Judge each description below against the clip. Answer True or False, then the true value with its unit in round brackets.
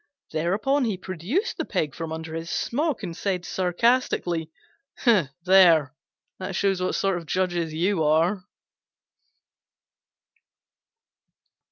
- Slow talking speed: True (110 wpm)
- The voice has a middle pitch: True (180 Hz)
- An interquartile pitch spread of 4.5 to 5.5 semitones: False (3.4 semitones)